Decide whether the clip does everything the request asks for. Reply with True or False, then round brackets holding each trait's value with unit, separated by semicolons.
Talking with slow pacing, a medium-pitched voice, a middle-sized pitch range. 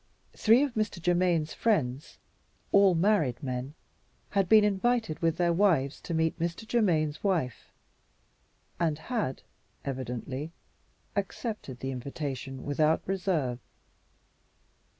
False (110 wpm; 165 Hz; 6.6 semitones)